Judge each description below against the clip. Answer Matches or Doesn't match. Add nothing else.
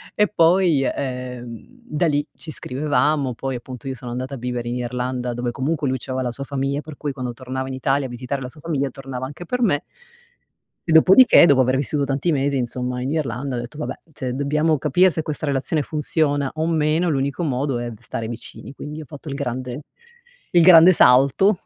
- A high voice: Doesn't match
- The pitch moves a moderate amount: Matches